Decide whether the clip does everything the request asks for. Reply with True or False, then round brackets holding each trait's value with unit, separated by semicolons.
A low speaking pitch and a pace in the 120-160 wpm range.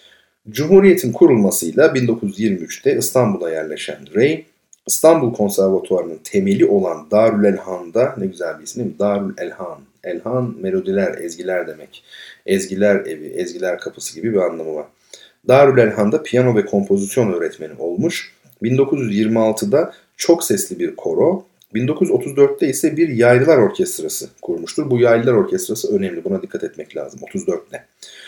True (120 Hz; 125 wpm)